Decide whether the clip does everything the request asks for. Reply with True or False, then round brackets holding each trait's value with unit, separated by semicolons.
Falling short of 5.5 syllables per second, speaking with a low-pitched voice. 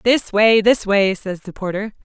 False (4.3 syllables/s; 205 Hz)